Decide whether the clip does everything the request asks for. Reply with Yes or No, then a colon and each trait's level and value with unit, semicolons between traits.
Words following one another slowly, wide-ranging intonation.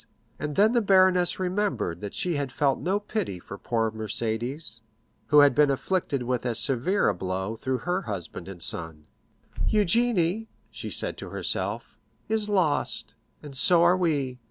No: average, 160 wpm; wide, 8.8 semitones